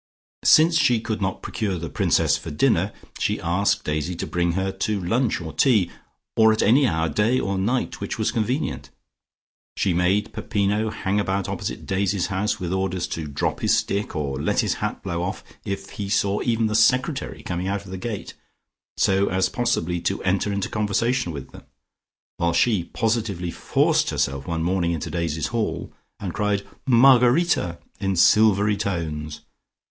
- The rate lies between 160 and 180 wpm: Yes, average, 170 wpm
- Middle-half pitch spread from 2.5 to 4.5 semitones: Yes, average, 3.9 semitones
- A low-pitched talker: Yes, low, 100 Hz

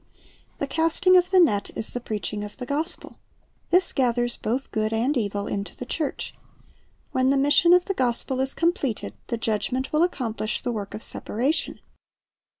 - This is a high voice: Yes, very high, 255 Hz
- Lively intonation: Yes, wide, 6.0 semitones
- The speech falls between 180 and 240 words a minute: No, average, 170 wpm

